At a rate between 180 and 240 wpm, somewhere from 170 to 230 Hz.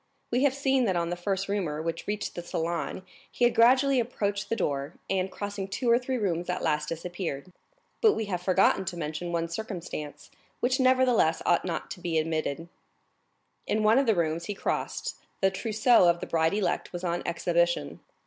Yes: average, 190 wpm; medium, 185 Hz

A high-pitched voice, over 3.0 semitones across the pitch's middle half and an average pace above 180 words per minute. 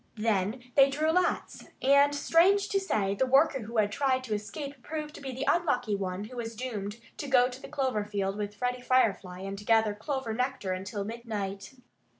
Yes: high, 245 Hz; average, 4.8 semitones; average, 190 wpm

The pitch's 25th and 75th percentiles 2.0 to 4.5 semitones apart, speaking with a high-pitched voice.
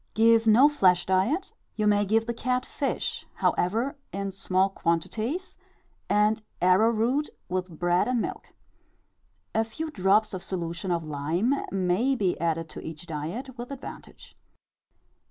No: average, 4.9 semitones; high, 205 Hz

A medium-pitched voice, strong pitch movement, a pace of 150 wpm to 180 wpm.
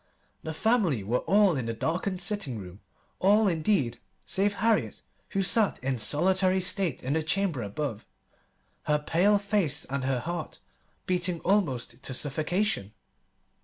No: medium, 165 Hz; wide, 6.9 semitones; average, 140 wpm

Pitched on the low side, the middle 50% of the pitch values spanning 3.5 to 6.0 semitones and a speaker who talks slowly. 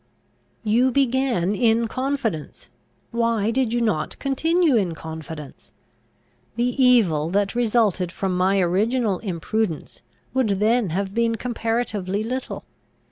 No: high, 225 Hz; average, 4.5 semitones; slow, 115 wpm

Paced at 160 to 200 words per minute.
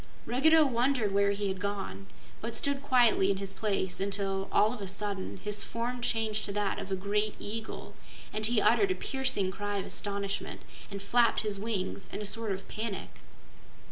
Yes: average, 185 wpm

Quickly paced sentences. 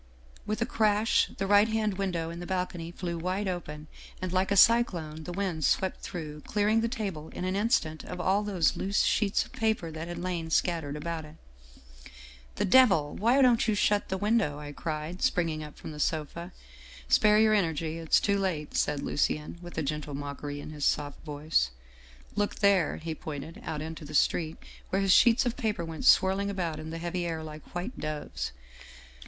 Yes: fast, 210 wpm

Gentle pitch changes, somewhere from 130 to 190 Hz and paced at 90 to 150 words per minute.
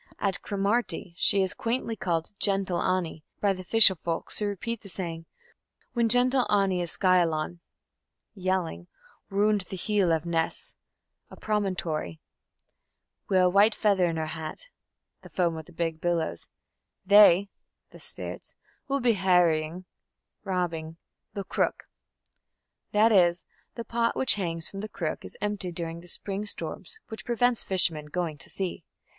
No: average, 3.7 semitones; medium, 185 Hz; average, 145 wpm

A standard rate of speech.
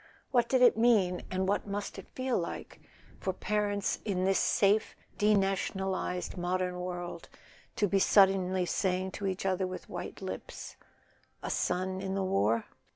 Yes: average, 155 wpm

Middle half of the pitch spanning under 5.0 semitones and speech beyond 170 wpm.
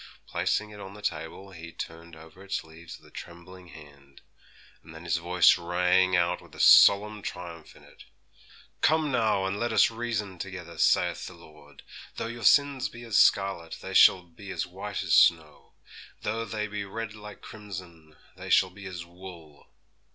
Yes: average, 3.8 semitones; average, 180 wpm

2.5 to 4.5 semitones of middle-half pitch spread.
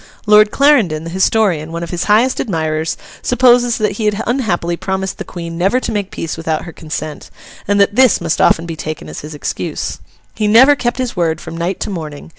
No: average, 5.3 semitones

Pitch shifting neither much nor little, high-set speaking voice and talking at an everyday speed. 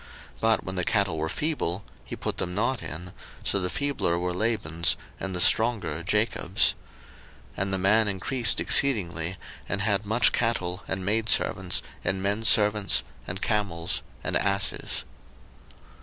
No: average, 3.7 semitones; low, 100 Hz; average, 145 wpm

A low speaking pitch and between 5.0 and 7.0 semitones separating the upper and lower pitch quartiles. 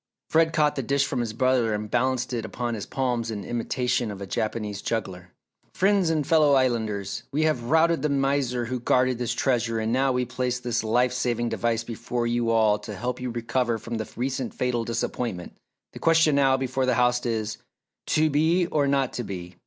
No: low, 125 Hz; average, 2.8 semitones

